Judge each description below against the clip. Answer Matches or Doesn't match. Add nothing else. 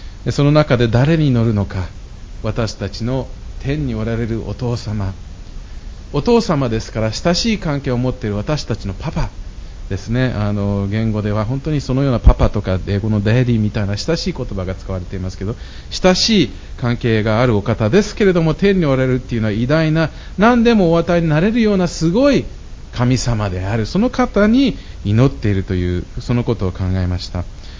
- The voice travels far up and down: Matches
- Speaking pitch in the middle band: Doesn't match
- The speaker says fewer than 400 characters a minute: Matches